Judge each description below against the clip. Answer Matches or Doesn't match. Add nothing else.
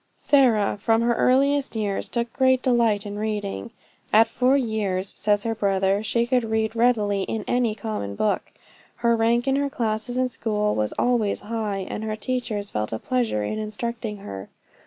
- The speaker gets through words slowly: Doesn't match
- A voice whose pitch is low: Doesn't match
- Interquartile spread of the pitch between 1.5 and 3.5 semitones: Matches